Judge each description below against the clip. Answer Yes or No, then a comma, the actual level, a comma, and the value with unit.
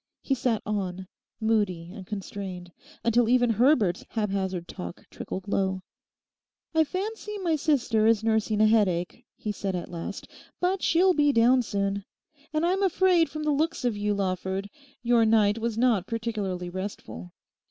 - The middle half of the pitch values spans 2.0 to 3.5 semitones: No, average, 5.1 semitones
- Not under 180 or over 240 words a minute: No, average, 155 wpm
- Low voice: No, high, 220 Hz